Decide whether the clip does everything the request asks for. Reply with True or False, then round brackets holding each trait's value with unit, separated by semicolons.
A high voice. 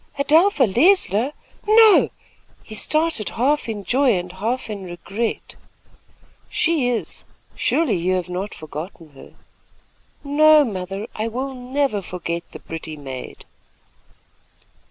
True (225 Hz)